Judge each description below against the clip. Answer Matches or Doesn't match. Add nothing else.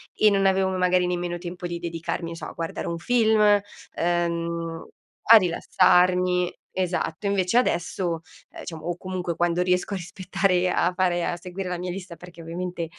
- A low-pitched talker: Doesn't match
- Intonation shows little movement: Matches